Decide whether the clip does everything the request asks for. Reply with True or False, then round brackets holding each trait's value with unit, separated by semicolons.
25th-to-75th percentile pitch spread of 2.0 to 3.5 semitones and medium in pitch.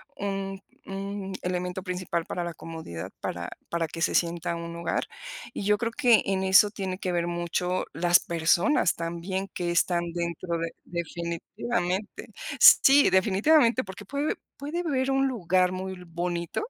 True (2.8 semitones; 180 Hz)